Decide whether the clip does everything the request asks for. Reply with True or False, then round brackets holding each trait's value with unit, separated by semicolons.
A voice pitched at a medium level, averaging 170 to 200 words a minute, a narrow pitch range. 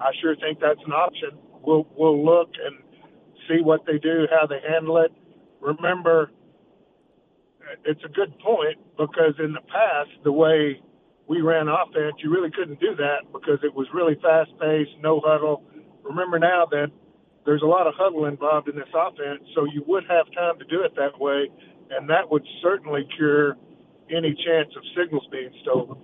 True (155 Hz; 180 wpm; 2.1 semitones)